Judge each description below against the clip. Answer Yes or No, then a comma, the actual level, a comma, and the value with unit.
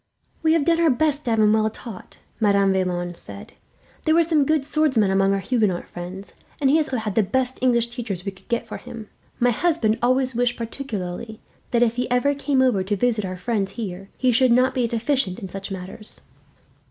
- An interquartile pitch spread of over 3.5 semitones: Yes, average, 4.9 semitones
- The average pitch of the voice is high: Yes, high, 230 Hz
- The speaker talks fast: Yes, fast, 215 wpm